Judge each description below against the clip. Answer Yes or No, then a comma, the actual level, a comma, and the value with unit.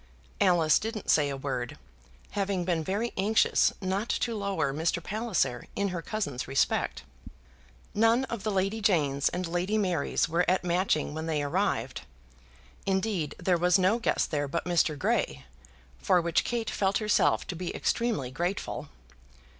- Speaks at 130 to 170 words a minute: Yes, average, 155 wpm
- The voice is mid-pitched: Yes, medium, 180 Hz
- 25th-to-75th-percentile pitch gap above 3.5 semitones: Yes, average, 4.7 semitones